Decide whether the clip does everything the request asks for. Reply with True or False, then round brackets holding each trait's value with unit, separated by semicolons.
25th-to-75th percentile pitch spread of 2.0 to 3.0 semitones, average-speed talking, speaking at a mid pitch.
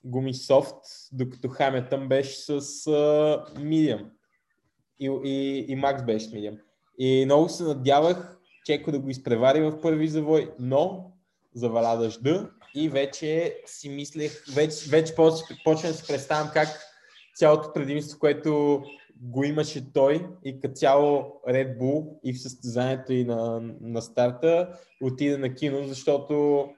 True (2.7 semitones; 140 wpm; 145 Hz)